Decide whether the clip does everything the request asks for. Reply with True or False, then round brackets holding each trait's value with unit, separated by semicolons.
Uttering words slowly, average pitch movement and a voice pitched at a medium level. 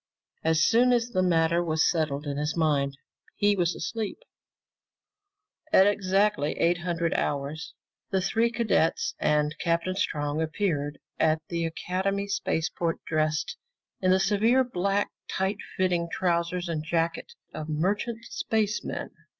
True (125 wpm; 4.2 semitones; 175 Hz)